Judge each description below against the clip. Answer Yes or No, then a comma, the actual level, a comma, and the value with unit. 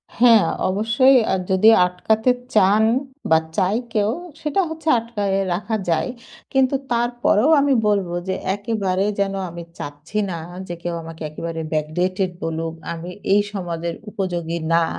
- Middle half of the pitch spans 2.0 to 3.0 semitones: No, average, 4.6 semitones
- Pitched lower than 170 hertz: No, high, 195 Hz